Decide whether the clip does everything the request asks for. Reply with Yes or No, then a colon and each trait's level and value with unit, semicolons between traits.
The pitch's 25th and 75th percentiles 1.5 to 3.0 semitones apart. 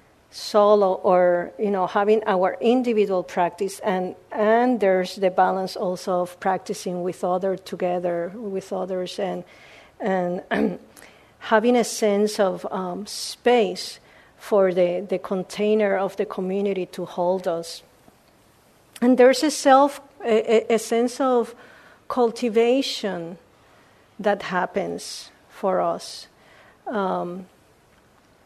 No: average, 3.6 semitones